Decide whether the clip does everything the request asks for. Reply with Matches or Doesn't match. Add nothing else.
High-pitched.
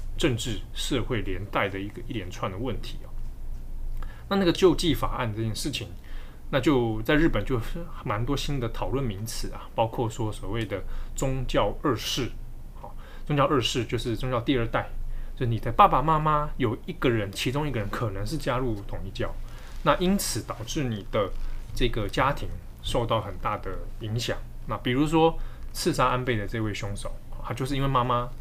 Doesn't match